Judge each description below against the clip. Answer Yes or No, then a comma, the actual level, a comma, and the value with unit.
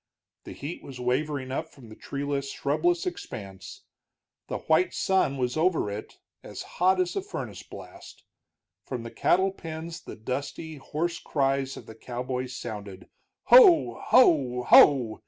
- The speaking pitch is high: No, medium, 140 Hz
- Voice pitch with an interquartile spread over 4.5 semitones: Yes, average, 5.1 semitones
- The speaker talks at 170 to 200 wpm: No, average, 145 wpm